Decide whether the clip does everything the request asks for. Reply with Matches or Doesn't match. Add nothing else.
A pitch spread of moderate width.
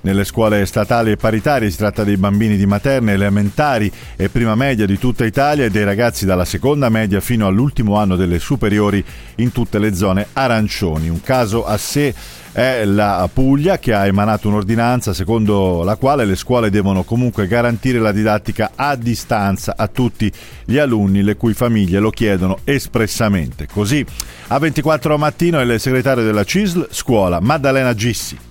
Matches